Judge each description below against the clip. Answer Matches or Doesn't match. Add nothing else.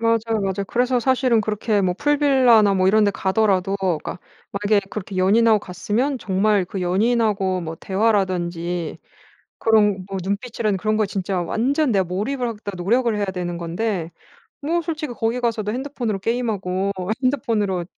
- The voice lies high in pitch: Matches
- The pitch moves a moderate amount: Matches